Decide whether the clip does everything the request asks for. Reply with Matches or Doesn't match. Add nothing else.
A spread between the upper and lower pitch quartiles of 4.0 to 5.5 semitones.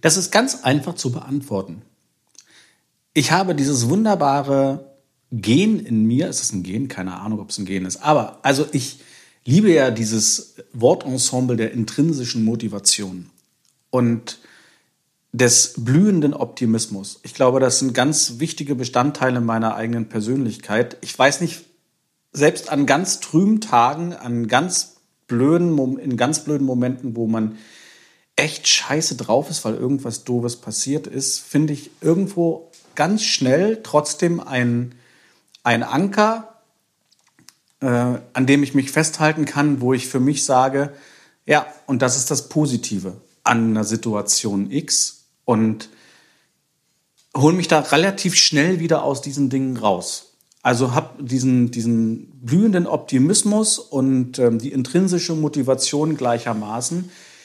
Matches